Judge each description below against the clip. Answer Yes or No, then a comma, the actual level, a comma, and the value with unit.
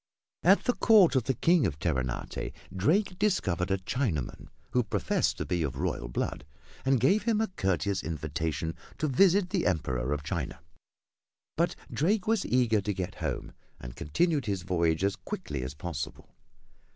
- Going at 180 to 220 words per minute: No, average, 165 wpm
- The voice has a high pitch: No, low, 100 Hz